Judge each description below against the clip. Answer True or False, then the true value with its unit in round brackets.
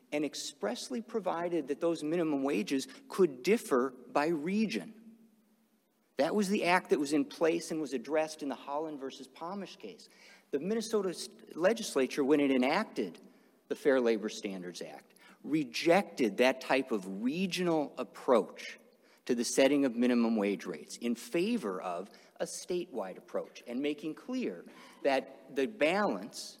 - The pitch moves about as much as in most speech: False (7.2 semitones)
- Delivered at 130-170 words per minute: True (145 wpm)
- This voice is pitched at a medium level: True (155 Hz)